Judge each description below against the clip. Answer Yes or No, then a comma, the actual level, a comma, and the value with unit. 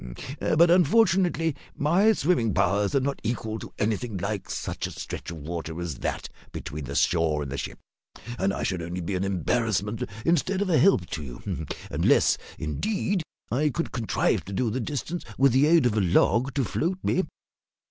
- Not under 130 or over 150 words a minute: No, average, 185 wpm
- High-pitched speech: No, low, 115 Hz